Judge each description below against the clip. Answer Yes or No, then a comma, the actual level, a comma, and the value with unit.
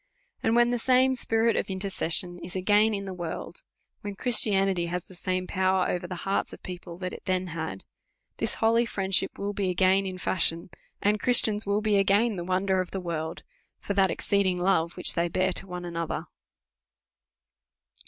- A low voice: No, high, 190 Hz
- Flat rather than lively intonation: Yes, narrow, 2.3 semitones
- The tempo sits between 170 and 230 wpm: Yes, average, 185 wpm